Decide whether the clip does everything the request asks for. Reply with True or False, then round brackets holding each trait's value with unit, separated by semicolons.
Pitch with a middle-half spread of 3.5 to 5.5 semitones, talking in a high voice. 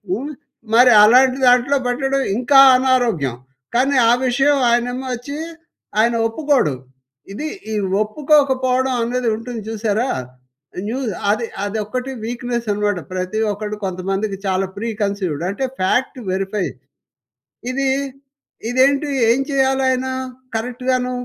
True (3.8 semitones; 245 Hz)